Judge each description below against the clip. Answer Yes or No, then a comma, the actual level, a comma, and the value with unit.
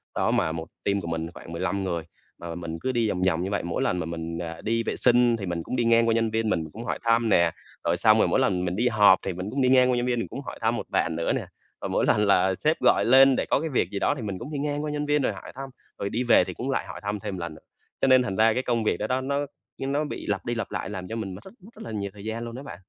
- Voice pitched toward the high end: No, low, 110 Hz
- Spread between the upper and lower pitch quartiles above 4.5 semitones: Yes, wide, 5.5 semitones